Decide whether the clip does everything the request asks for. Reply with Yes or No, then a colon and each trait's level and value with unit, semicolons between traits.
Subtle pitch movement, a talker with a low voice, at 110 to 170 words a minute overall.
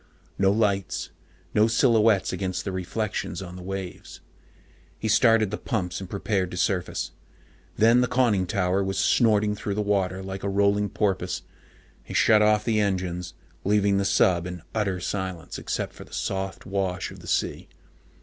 Yes: narrow, 2.3 semitones; low, 100 Hz; average, 165 wpm